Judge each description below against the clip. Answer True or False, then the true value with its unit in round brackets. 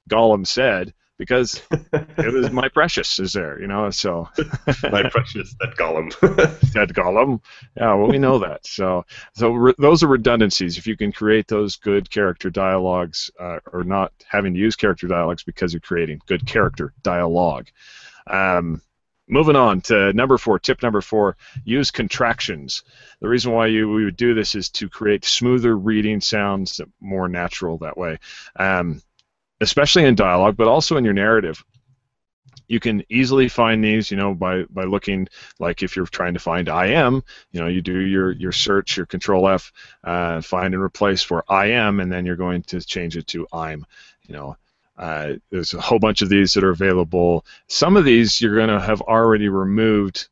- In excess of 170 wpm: True (180 wpm)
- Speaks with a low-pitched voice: True (100 Hz)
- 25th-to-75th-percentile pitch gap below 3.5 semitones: False (3.9 semitones)